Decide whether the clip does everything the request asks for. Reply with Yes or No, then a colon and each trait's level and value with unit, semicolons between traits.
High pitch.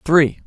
No: medium, 155 Hz